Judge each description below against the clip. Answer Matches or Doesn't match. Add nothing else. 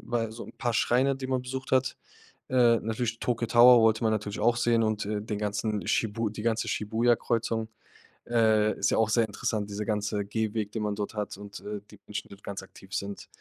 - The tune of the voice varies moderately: Doesn't match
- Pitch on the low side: Matches